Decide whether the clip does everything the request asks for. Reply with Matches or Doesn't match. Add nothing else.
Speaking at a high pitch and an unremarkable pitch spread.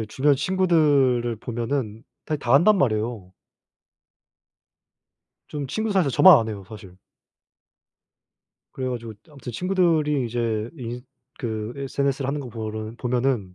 Doesn't match